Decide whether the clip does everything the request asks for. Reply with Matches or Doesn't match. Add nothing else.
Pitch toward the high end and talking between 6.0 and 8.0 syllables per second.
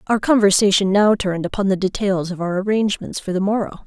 Matches